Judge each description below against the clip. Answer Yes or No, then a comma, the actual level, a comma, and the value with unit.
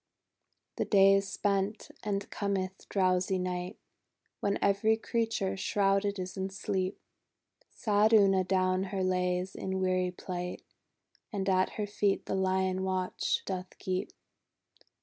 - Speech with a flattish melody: Yes, narrow, 1.3 semitones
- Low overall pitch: No, high, 190 Hz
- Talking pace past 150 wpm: No, slow, 135 wpm